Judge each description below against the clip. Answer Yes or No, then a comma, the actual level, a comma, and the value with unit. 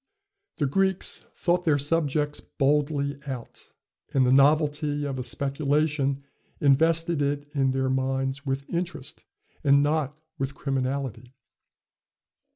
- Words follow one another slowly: Yes, slow, 115 wpm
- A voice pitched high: No, medium, 140 Hz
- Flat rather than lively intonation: Yes, narrow, 2.1 semitones